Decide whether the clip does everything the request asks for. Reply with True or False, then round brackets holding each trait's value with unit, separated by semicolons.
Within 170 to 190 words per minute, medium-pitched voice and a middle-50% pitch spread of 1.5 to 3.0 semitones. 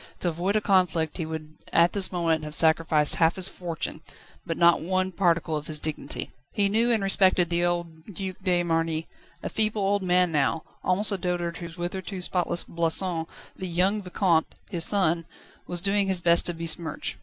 True (185 wpm; 175 Hz; 2.4 semitones)